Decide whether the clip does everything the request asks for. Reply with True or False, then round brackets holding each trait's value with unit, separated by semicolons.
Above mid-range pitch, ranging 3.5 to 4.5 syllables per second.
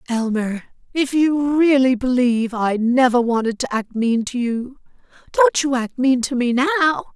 True (255 Hz; 4.3 syllables/s)